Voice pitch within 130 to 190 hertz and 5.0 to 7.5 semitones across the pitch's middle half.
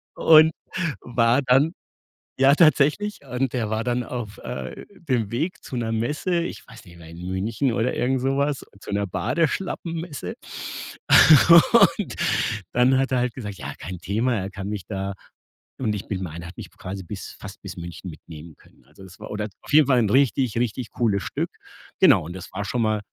No: low, 115 Hz; wide, 5.5 semitones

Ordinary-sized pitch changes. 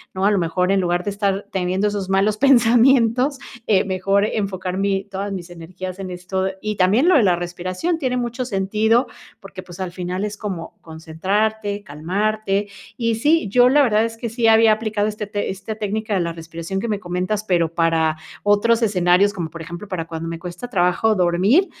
Yes: average, 3.3 semitones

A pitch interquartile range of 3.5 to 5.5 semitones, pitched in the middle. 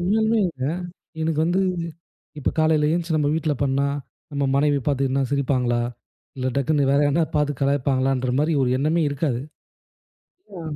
No: average, 2.9 semitones; medium, 145 Hz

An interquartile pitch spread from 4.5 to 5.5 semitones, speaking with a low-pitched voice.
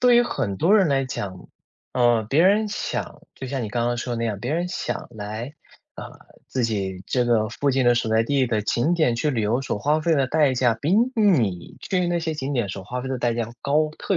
Yes: average, 5.1 semitones; low, 125 Hz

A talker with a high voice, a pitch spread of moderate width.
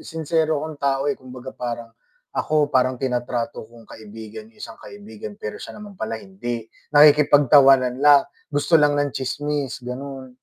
No: low, 130 Hz; average, 3.9 semitones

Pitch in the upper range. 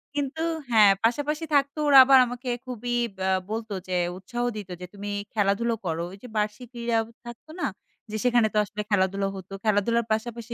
Yes: high, 230 Hz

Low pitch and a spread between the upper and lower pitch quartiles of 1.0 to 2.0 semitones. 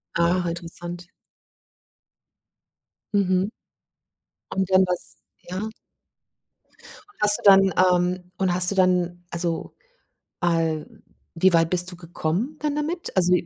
No: medium, 180 Hz; narrow, 1.7 semitones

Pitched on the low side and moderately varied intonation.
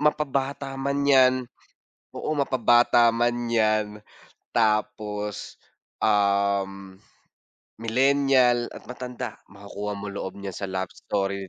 Yes: low, 110 Hz; average, 4.3 semitones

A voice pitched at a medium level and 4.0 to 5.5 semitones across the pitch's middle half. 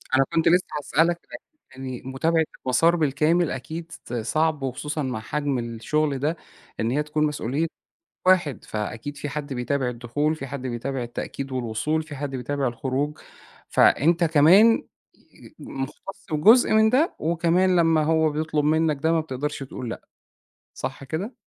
No: medium, 150 Hz; average, 3.6 semitones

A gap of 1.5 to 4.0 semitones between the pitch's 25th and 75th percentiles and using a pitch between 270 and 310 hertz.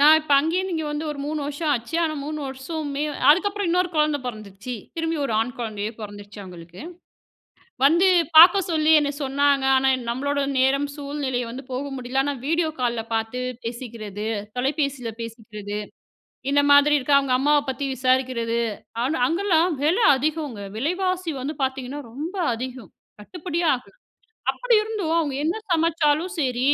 No: average, 4.4 semitones; very high, 285 Hz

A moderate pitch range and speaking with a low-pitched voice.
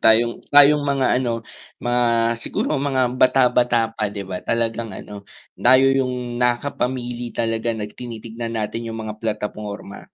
No: narrow, 2.1 semitones; low, 120 Hz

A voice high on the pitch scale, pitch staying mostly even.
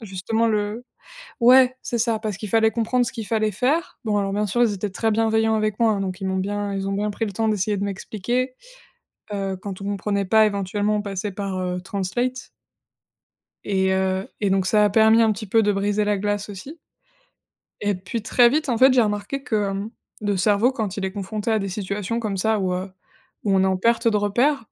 Yes: high, 210 Hz; narrow, 2.3 semitones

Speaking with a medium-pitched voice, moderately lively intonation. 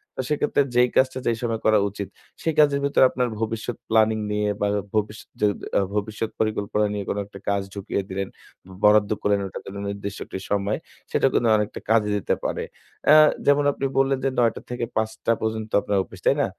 No: low, 110 Hz; average, 3.1 semitones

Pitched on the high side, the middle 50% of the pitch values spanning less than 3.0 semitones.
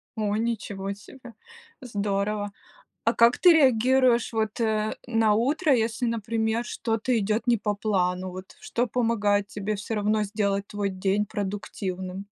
Yes: high, 215 Hz; narrow, 2.4 semitones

